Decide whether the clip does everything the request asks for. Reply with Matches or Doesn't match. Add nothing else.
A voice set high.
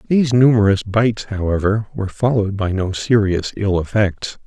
Doesn't match